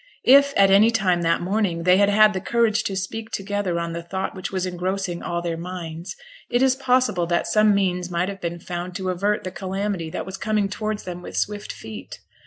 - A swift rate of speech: Yes, fast, 215 wpm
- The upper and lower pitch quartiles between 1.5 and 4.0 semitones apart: Yes, average, 3.0 semitones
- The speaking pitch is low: No, high, 190 Hz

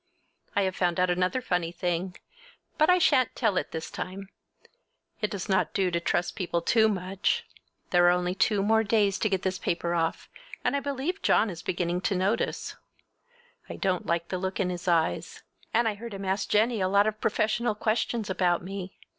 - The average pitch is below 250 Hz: Yes, high, 190 Hz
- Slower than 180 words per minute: No, average, 195 wpm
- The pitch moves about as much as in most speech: Yes, average, 3.3 semitones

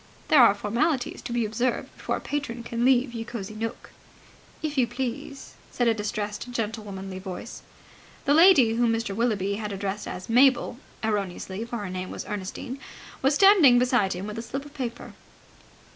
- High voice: Yes, high, 230 Hz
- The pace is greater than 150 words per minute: Yes, average, 175 wpm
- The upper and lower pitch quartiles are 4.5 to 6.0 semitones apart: No, average, 3.4 semitones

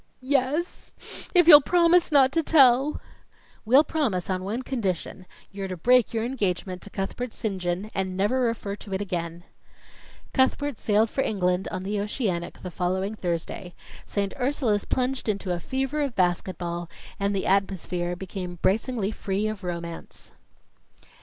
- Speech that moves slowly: No, average, 155 wpm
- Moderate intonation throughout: No, wide, 5.7 semitones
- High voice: Yes, high, 200 Hz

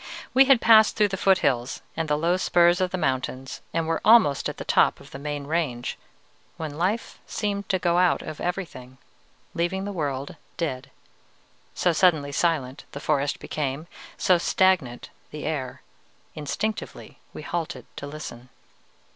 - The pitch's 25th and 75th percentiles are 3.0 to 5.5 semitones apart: Yes, average, 4.7 semitones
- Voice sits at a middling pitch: Yes, medium, 160 Hz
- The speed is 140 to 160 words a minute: Yes, average, 155 wpm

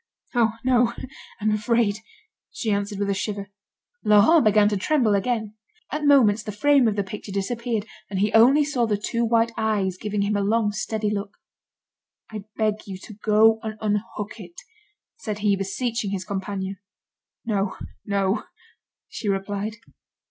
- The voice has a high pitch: Yes, high, 210 Hz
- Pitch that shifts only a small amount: Yes, narrow, 2.2 semitones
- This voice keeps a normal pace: Yes, average, 155 wpm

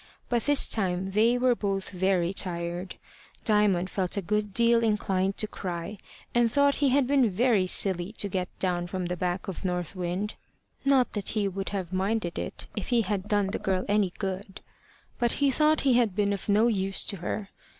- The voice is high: Yes, high, 200 Hz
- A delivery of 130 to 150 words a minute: No, average, 195 wpm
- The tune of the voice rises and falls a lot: No, average, 3.5 semitones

